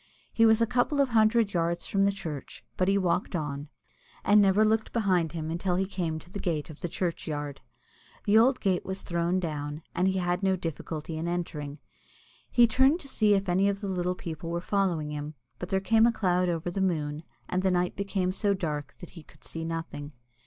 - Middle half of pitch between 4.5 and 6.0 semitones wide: No, average, 3.5 semitones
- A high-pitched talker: No, medium, 180 Hz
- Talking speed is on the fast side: Yes, fast, 215 wpm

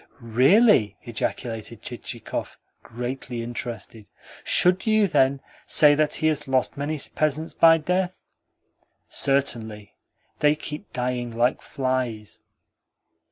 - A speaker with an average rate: No, slow, 105 wpm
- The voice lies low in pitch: Yes, low, 130 Hz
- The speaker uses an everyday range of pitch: Yes, average, 4.5 semitones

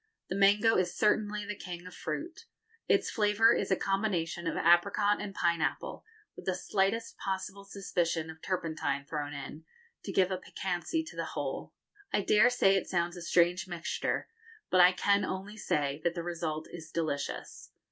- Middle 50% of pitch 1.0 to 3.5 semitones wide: Yes, average, 3.2 semitones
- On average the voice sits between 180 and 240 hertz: Yes, medium, 185 Hz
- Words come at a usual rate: Yes, average, 170 wpm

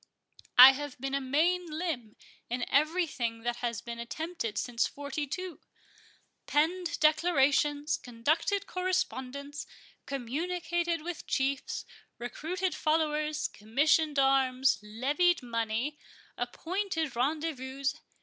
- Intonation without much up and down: No, average, 4.4 semitones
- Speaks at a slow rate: Yes, slow, 100 wpm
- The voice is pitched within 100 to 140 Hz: No, very high, 290 Hz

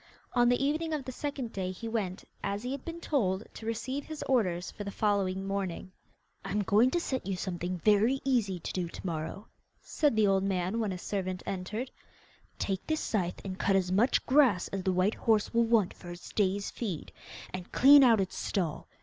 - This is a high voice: Yes, high, 200 Hz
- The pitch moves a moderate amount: Yes, average, 4.7 semitones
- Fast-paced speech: Yes, fast, 210 wpm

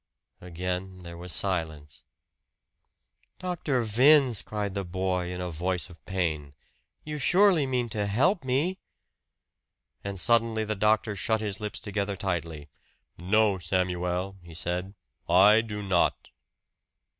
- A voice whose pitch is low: Yes, very low, 95 Hz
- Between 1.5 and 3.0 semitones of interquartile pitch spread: No, average, 3.7 semitones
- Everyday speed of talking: No, slow, 125 wpm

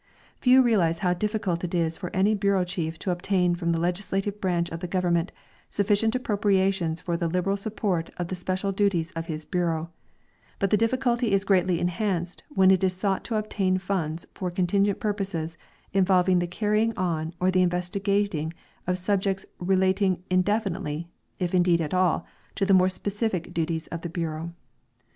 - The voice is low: No, medium, 185 Hz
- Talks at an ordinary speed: Yes, average, 170 wpm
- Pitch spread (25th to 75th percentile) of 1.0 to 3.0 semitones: Yes, narrow, 2.5 semitones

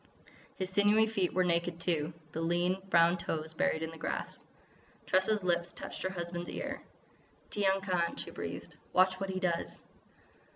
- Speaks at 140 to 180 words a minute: Yes, average, 160 wpm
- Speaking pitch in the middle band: Yes, medium, 180 Hz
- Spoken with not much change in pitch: Yes, narrow, 1.9 semitones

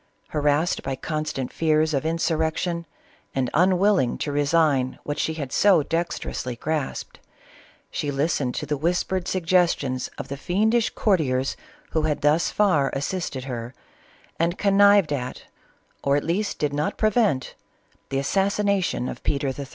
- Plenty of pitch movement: No, average, 4.5 semitones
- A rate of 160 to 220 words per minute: No, average, 145 wpm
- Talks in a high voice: No, medium, 155 Hz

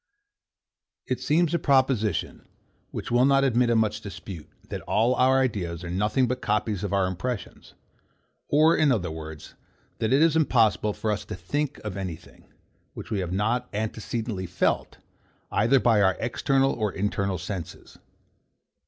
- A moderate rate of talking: Yes, average, 160 wpm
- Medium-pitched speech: No, low, 110 Hz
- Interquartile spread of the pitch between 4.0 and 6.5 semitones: Yes, average, 5.1 semitones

